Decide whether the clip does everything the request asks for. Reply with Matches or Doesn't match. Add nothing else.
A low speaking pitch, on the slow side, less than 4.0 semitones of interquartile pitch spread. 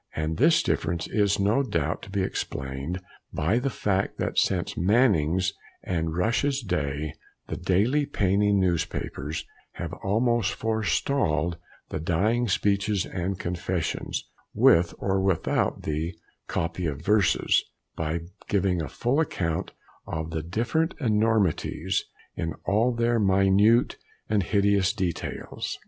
Doesn't match